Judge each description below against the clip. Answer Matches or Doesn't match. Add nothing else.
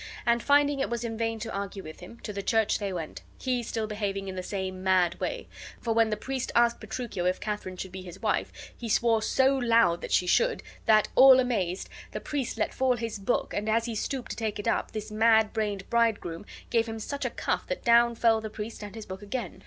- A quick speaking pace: Matches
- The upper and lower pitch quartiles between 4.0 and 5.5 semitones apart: Doesn't match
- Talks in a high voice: Matches